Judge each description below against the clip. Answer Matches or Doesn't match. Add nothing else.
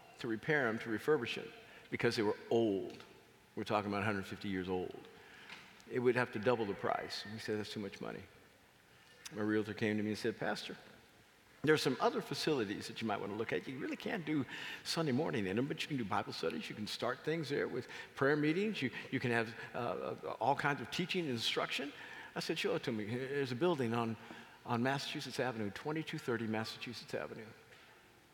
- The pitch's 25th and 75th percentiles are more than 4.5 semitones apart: Matches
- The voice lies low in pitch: Matches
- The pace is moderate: Doesn't match